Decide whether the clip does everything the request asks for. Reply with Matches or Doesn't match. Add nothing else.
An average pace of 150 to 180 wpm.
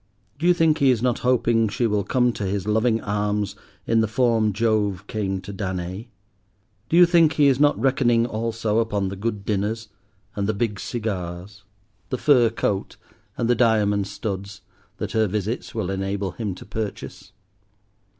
Matches